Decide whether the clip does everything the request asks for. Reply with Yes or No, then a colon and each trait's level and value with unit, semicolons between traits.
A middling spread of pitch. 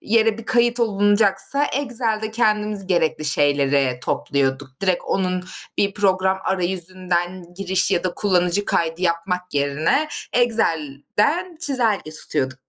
Yes: average, 4.5 semitones